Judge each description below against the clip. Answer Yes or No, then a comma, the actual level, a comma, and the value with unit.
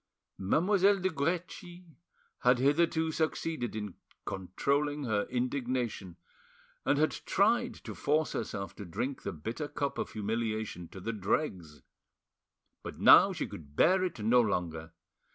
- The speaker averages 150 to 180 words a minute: No, slow, 135 wpm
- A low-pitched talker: Yes, low, 125 Hz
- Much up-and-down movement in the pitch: Yes, wide, 7.8 semitones